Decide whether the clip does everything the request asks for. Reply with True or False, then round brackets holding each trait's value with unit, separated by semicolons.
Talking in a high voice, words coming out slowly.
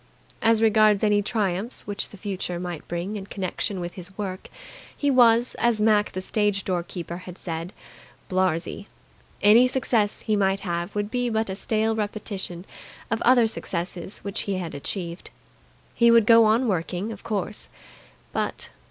False (205 Hz; 160 wpm)